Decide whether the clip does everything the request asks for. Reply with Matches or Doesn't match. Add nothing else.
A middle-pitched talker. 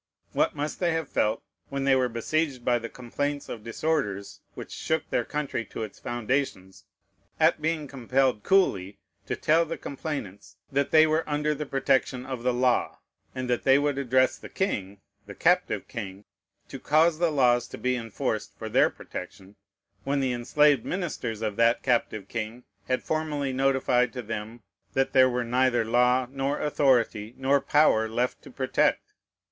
Doesn't match